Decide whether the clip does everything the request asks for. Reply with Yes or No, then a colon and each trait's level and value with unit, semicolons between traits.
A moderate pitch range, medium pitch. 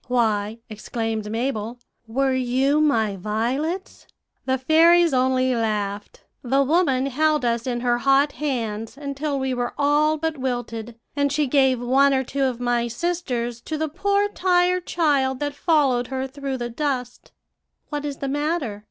No: average, 3.6 semitones; very high, 265 Hz